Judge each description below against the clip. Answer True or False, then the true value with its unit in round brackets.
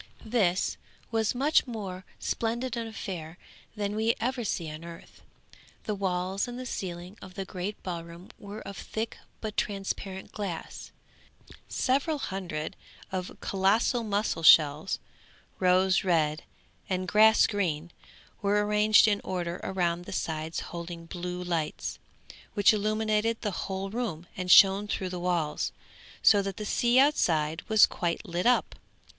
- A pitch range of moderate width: True (3.6 semitones)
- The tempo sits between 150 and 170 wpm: False (140 wpm)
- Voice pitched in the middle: False (195 Hz)